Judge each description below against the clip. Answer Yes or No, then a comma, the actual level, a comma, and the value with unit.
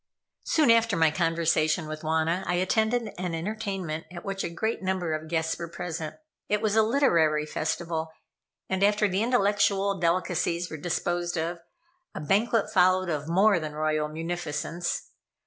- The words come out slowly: No, average, 155 wpm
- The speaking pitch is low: No, medium, 175 Hz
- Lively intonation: No, average, 3.7 semitones